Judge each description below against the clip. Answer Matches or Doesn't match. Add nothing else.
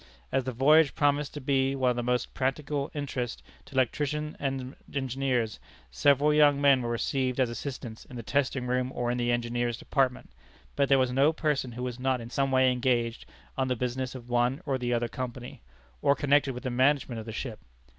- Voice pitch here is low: Matches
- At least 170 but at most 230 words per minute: Matches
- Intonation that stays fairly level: Matches